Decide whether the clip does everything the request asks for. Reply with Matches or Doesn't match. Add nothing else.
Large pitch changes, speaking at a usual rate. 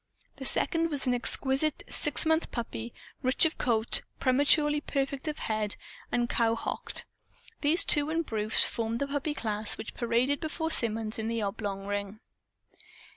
Doesn't match